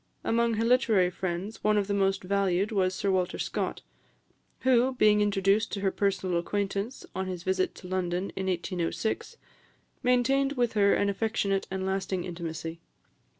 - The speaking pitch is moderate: No, high, 195 Hz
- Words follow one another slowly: No, average, 155 wpm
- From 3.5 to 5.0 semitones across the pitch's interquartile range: No, average, 2.7 semitones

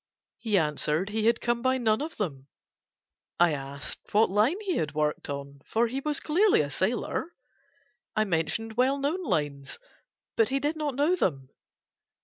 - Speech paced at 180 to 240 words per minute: No, average, 165 wpm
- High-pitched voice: Yes, high, 220 Hz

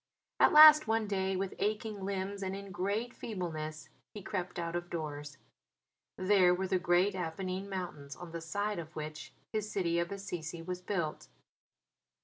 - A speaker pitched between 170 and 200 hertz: Yes, medium, 185 Hz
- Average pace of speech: Yes, average, 160 wpm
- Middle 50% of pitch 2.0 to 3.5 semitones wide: Yes, average, 2.9 semitones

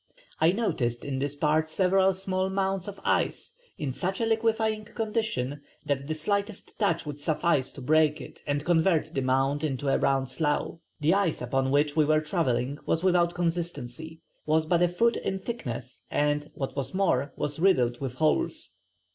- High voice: No, medium, 155 Hz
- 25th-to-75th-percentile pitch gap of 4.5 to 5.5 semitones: Yes, average, 5.1 semitones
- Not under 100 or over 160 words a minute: No, average, 175 wpm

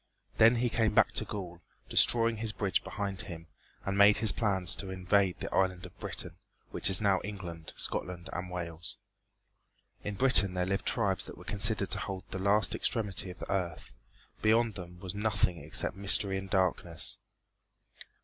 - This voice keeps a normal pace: Yes, average, 170 wpm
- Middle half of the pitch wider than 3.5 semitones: No, narrow, 2.5 semitones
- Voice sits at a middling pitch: No, very low, 95 Hz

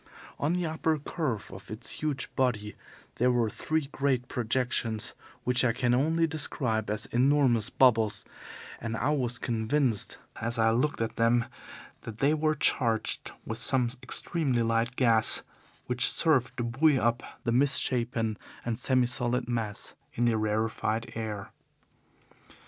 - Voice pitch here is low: Yes, low, 120 Hz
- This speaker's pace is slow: No, average, 145 wpm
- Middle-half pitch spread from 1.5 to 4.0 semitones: Yes, average, 2.9 semitones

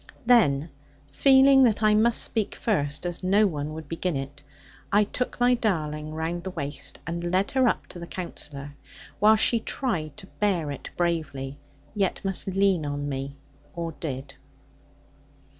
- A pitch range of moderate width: No, wide, 6.2 semitones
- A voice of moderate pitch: Yes, medium, 175 Hz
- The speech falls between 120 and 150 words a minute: No, average, 160 wpm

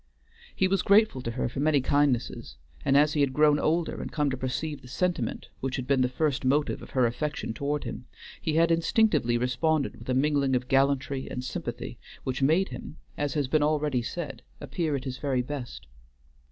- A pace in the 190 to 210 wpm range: Yes, average, 200 wpm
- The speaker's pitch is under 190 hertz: Yes, medium, 140 Hz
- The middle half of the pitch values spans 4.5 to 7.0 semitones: No, average, 2.9 semitones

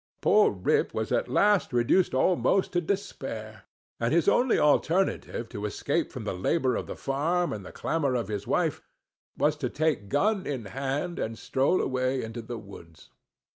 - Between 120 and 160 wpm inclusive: No, average, 170 wpm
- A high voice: No, low, 135 Hz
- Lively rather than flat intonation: Yes, wide, 7.4 semitones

